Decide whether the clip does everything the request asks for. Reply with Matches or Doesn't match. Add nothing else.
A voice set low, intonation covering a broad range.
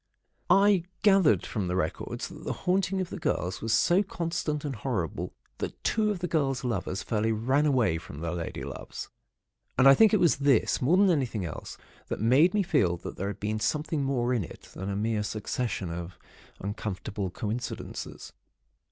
Matches